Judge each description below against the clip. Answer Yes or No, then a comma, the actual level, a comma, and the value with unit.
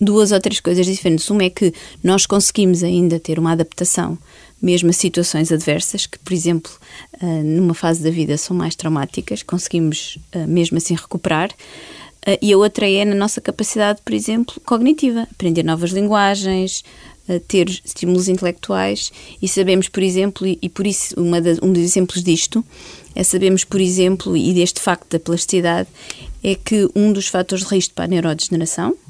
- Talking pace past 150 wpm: Yes, average, 165 wpm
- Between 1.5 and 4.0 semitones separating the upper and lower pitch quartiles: Yes, average, 2.7 semitones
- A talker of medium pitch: Yes, medium, 180 Hz